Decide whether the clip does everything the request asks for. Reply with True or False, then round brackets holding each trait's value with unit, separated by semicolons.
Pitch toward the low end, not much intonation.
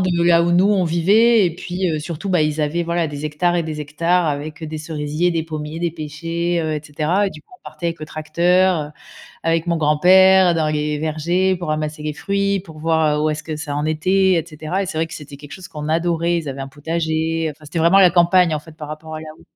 False (160 Hz; 2.3 semitones)